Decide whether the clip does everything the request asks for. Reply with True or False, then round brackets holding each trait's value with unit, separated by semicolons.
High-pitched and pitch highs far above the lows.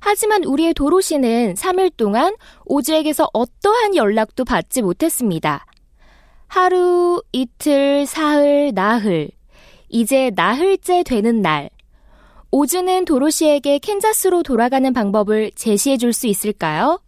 True (285 Hz; 7.9 semitones)